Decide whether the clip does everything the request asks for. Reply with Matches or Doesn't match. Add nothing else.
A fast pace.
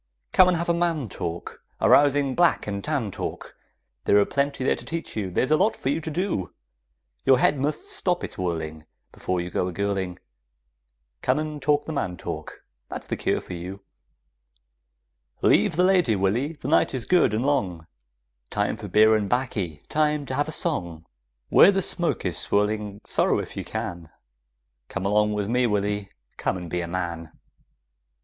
Doesn't match